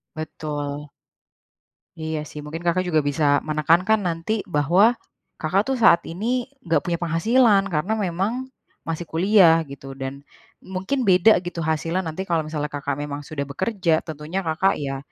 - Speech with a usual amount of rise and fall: Yes, average, 4.1 semitones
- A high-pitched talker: No, medium, 165 Hz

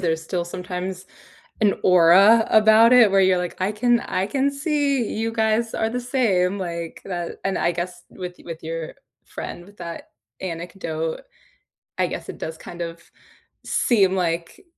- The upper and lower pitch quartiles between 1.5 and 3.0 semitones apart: No, average, 4.4 semitones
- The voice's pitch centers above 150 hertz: Yes, medium, 185 Hz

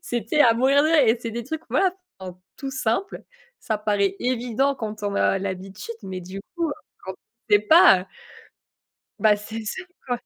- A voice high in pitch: Yes, high, 225 Hz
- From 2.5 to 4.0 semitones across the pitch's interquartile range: No, average, 4.9 semitones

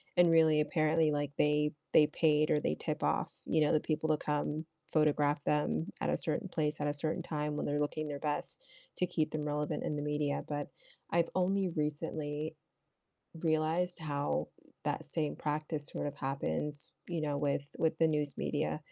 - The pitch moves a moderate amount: No, narrow, 1.3 semitones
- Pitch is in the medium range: Yes, medium, 150 Hz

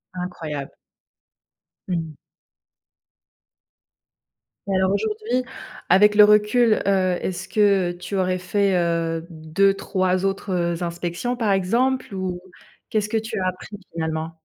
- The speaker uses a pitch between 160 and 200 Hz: Yes, medium, 185 Hz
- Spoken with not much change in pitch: No, average, 3.2 semitones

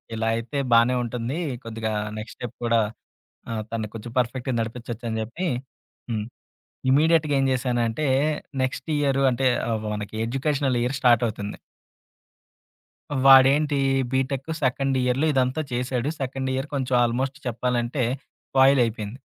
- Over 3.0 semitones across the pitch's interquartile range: No, narrow, 2.6 semitones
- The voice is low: Yes, low, 125 Hz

